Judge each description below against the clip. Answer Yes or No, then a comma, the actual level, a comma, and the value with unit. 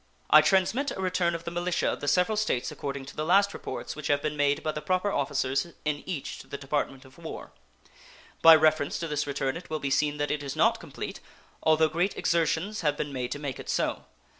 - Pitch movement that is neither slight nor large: Yes, average, 3.4 semitones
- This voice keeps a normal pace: No, fast, 230 wpm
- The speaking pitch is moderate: Yes, medium, 155 Hz